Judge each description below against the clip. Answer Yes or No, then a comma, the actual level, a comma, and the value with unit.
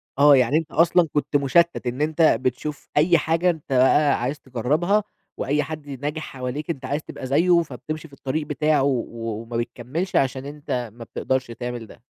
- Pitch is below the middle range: No, medium, 145 Hz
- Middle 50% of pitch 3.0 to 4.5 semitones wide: Yes, average, 3.6 semitones